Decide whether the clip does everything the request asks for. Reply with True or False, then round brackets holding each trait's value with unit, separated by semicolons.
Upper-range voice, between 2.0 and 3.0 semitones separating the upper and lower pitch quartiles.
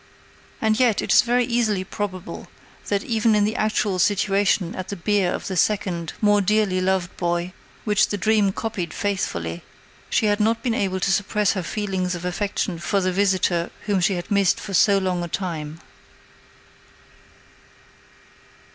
True (195 Hz; 2.6 semitones)